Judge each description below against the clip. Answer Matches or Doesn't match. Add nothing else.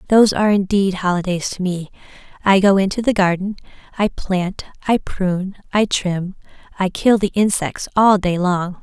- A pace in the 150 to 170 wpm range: Matches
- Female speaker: Matches